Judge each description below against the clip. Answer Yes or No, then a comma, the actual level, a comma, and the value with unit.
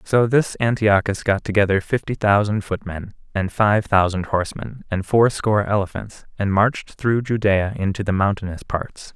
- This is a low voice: Yes, low, 105 Hz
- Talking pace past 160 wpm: No, average, 150 wpm